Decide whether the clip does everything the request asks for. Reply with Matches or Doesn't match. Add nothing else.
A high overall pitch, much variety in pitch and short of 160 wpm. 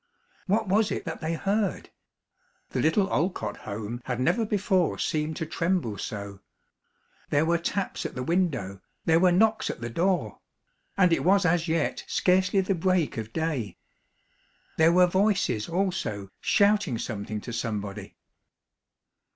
Doesn't match